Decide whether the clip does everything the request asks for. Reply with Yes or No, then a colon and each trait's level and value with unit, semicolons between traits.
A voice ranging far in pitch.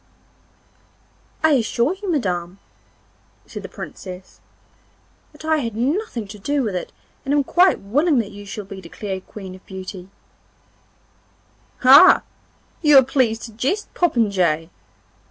Yes: wide, 7.2 semitones